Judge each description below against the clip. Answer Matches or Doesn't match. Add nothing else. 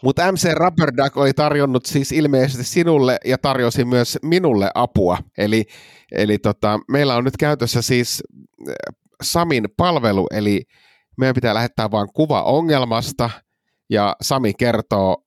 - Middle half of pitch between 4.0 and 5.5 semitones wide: Matches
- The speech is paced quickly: Doesn't match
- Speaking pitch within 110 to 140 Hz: Matches